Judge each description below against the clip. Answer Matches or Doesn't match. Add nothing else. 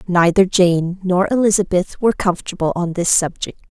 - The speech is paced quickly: Doesn't match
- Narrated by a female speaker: Matches